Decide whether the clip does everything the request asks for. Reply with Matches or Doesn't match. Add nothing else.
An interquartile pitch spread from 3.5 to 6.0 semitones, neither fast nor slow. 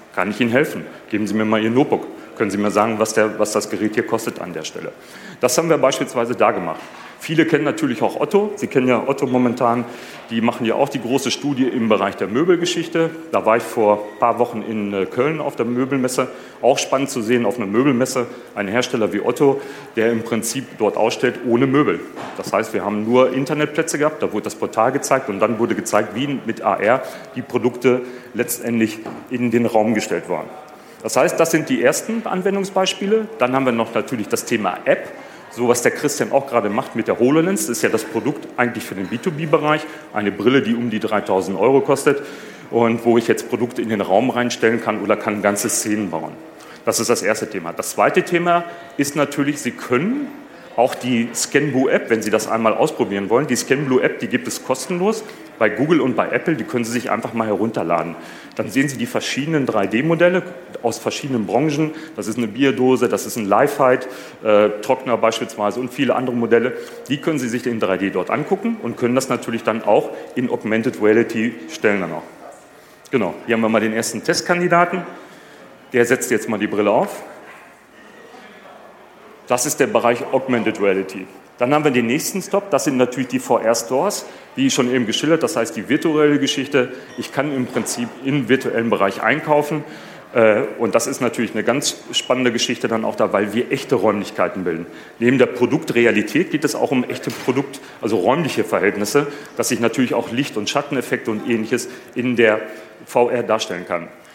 Doesn't match